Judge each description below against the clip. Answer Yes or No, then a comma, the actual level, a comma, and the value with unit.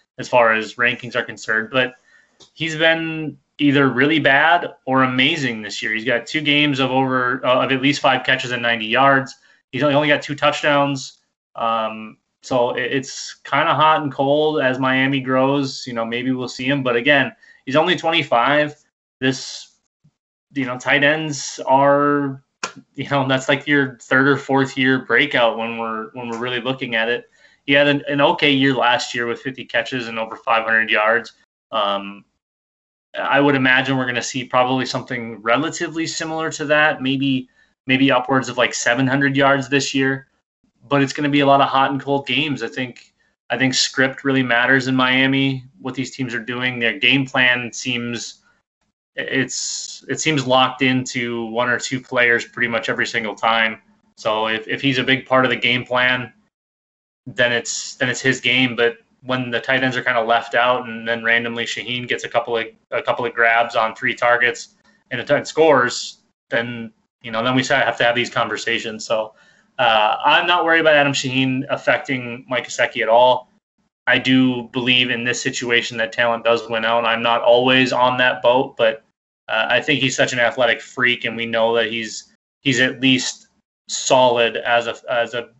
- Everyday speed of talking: Yes, average, 190 wpm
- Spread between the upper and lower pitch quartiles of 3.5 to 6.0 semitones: No, average, 2.7 semitones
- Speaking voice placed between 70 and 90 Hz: No, low, 130 Hz